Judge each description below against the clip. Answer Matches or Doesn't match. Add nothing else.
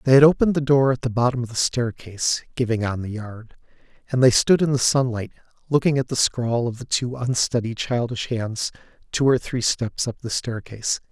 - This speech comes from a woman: Doesn't match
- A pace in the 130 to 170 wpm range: Doesn't match